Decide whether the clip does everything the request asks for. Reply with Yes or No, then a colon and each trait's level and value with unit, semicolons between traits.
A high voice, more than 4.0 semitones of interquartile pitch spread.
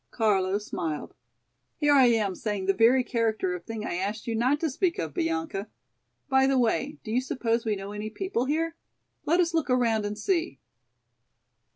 Yes: high, 225 Hz; average, 4.6 semitones